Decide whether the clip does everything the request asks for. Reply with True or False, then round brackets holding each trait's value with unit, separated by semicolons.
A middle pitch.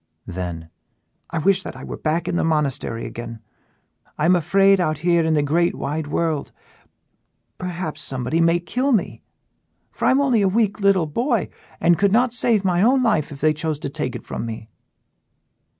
True (170 Hz)